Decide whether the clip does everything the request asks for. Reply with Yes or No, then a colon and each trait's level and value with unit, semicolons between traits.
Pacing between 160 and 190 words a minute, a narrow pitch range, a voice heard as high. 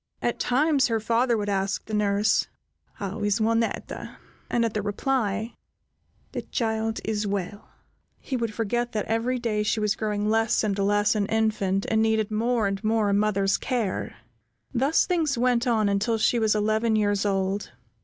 Yes: average, 170 wpm; narrow, 2.1 semitones; high, 220 Hz